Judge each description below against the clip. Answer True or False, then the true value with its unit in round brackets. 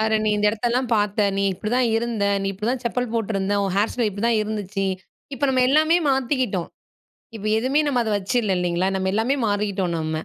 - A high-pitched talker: True (215 Hz)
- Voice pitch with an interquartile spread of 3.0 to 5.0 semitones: True (3.7 semitones)